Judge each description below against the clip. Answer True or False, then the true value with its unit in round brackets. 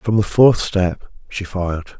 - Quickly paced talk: False (180 wpm)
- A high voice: False (95 Hz)